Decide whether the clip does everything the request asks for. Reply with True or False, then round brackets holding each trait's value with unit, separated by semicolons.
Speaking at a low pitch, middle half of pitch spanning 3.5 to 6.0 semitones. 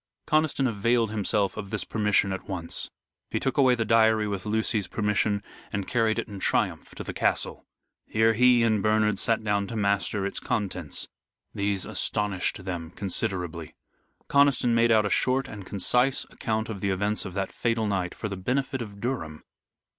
False (105 Hz; 2.7 semitones)